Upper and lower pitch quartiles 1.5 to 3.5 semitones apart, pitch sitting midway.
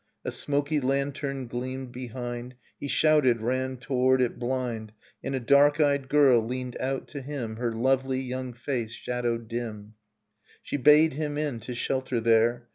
No: narrow, 2.4 semitones; low, 130 Hz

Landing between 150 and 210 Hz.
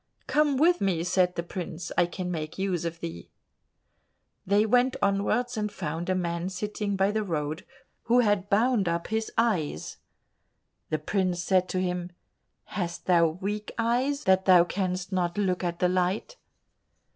Yes: medium, 185 Hz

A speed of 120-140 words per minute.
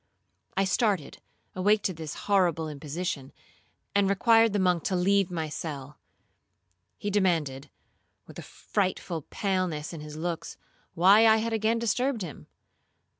Yes: slow, 135 wpm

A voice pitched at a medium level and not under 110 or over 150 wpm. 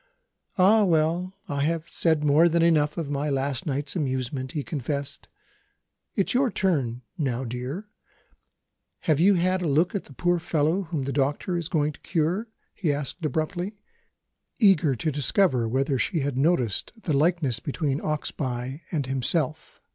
No: medium, 150 Hz; average, 160 wpm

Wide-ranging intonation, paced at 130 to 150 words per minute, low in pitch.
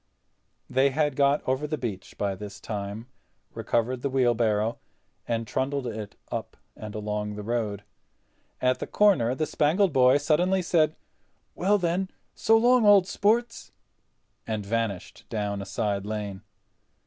Yes: wide, 6.8 semitones; average, 140 wpm; low, 125 Hz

